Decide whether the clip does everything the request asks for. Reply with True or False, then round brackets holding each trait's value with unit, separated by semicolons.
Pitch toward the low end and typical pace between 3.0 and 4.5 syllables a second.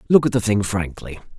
False (105 Hz; 5.7 syllables/s)